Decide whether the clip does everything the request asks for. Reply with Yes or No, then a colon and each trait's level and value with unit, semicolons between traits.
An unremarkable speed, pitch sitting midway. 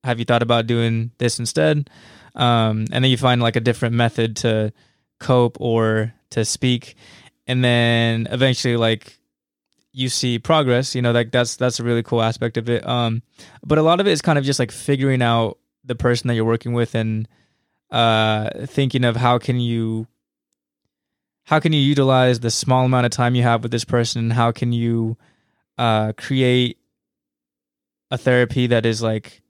No: average, 185 wpm; low, 120 Hz